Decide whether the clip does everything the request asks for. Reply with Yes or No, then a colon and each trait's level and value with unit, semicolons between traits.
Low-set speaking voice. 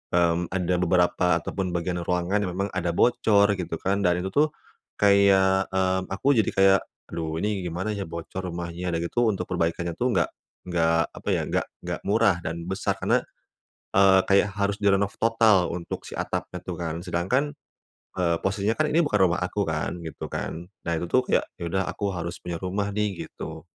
Yes: very low, 95 Hz